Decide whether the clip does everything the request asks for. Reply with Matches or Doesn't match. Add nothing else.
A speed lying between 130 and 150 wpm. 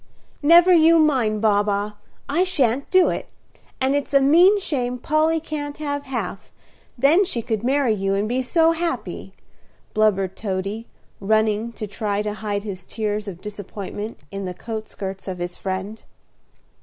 Doesn't match